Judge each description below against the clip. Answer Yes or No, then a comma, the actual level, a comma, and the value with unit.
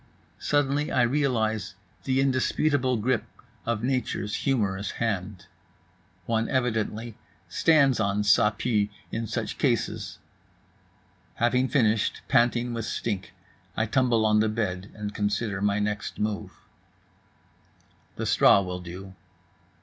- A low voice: Yes, low, 110 Hz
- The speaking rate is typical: No, slow, 115 wpm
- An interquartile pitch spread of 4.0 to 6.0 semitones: No, average, 3.4 semitones